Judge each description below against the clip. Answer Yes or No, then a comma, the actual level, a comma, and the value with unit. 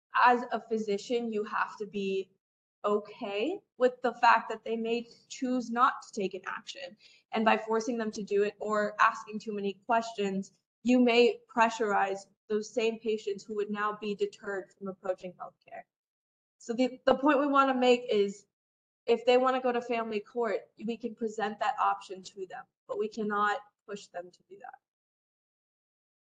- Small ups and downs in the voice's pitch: No, average, 3.1 semitones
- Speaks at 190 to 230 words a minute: No, average, 180 wpm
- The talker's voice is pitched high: Yes, high, 220 Hz